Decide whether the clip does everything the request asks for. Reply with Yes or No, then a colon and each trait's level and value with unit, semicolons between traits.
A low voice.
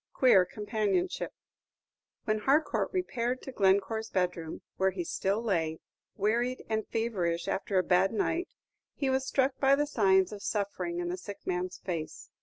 No: high, 205 Hz